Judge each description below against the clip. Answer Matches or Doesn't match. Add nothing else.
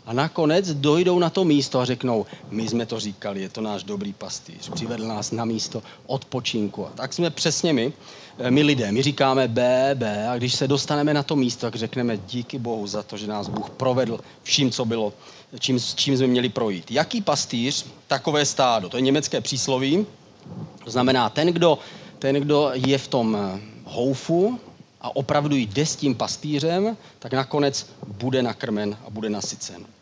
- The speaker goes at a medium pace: Doesn't match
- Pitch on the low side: Matches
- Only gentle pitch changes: Doesn't match